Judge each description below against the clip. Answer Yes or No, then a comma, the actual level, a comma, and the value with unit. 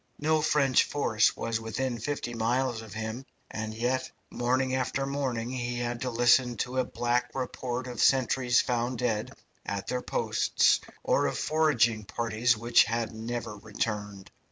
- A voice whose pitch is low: Yes, low, 120 Hz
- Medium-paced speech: Yes, average, 155 wpm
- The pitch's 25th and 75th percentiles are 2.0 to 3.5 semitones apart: Yes, narrow, 2.4 semitones